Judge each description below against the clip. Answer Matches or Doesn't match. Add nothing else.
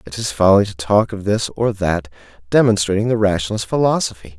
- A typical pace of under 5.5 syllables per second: Doesn't match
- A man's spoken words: Matches